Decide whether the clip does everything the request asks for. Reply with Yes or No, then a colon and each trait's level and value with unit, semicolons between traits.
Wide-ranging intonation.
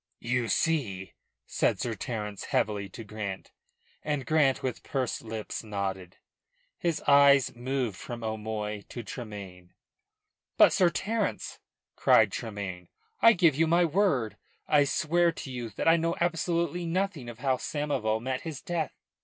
Yes: wide, 7.1 semitones